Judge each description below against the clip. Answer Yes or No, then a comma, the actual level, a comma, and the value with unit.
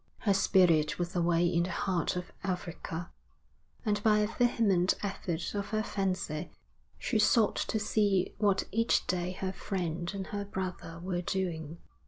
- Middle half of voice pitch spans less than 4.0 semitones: Yes, average, 2.8 semitones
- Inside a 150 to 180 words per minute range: Yes, average, 155 wpm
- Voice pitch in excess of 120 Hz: Yes, medium, 185 Hz